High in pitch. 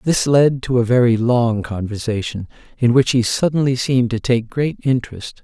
No: low, 120 Hz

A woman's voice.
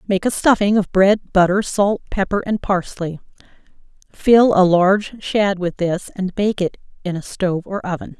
Yes: female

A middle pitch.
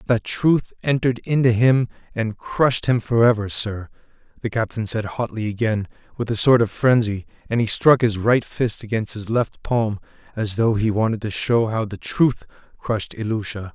No: low, 110 Hz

